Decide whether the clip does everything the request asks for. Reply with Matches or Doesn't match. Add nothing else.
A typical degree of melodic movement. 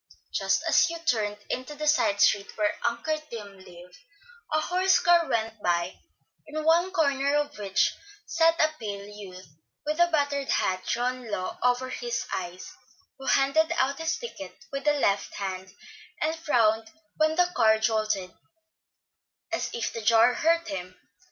Doesn't match